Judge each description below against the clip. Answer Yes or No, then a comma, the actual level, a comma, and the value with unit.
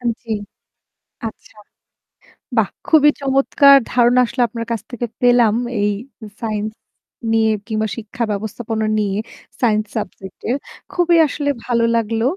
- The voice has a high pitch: Yes, high, 230 Hz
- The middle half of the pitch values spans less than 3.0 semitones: Yes, narrow, 2.4 semitones